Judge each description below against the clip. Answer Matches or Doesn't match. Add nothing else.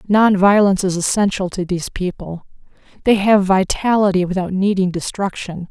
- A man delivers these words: Doesn't match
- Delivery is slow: Matches